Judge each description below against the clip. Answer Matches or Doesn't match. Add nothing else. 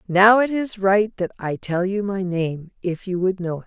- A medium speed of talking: Doesn't match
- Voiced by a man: Doesn't match